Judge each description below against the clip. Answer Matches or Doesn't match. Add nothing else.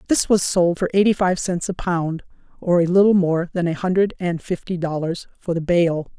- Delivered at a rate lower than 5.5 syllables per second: Matches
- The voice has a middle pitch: Matches